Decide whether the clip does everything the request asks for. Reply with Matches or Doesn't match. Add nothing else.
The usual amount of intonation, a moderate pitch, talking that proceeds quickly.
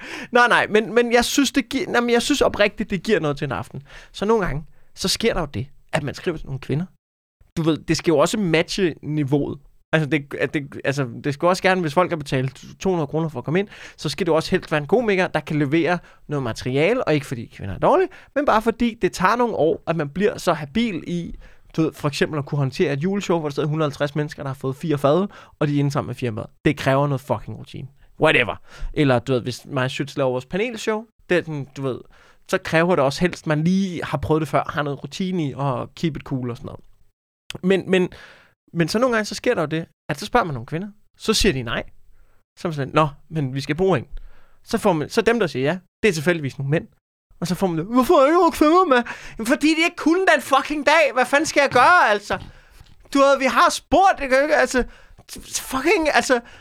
Doesn't match